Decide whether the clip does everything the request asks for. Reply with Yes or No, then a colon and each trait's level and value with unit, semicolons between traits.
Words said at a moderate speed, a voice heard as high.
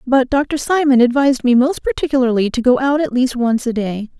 No: fast, 215 wpm; very high, 255 Hz